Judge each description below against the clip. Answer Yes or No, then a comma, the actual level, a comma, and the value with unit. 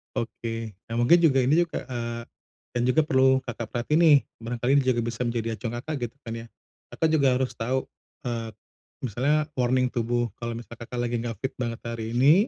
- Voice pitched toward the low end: Yes, low, 120 Hz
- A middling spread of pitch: No, narrow, 2.2 semitones